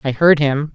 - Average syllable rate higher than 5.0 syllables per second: No, 4.6 syllables/s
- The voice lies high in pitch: No, medium, 145 Hz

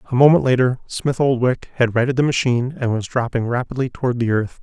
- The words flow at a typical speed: No, fast, 210 wpm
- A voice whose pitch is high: No, low, 125 Hz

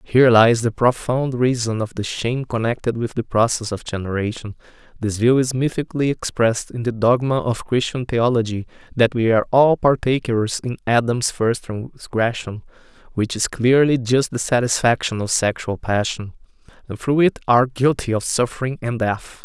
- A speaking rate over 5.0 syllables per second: No, 4.4 syllables/s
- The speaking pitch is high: No, low, 120 Hz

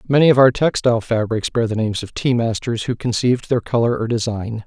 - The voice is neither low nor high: No, low, 115 Hz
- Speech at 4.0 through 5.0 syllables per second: No, 6.0 syllables/s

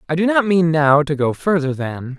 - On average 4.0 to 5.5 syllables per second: Yes, 5.0 syllables/s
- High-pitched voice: No, medium, 160 Hz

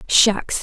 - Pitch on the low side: No, high, 205 Hz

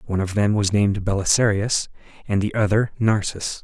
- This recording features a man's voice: Yes, male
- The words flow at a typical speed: Yes, average, 165 wpm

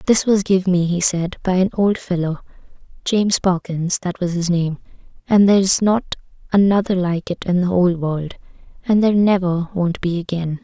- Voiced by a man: No, female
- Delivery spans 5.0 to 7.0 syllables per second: Yes, 5.1 syllables/s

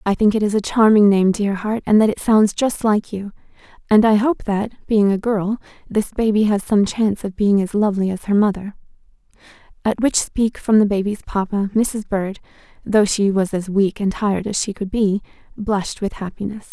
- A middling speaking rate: No, fast, 210 wpm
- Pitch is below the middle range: No, high, 205 Hz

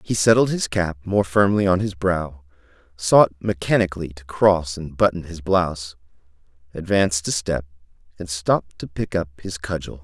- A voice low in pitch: Yes, very low, 85 Hz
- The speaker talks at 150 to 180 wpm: Yes, average, 160 wpm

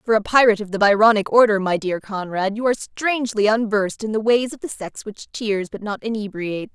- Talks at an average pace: No, fast, 220 wpm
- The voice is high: Yes, high, 215 Hz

